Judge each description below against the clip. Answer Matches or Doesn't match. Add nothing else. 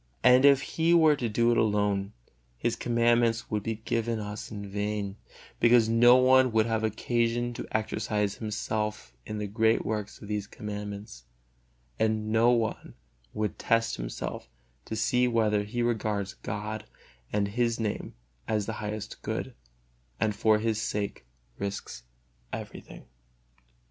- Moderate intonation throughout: Doesn't match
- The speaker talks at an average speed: Matches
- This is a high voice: Doesn't match